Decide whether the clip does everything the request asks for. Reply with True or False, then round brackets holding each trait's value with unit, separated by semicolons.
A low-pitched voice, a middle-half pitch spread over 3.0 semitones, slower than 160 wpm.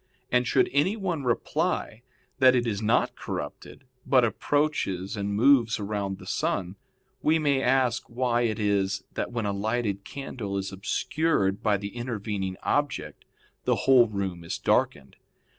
True (110 Hz; 4.7 semitones; 150 wpm)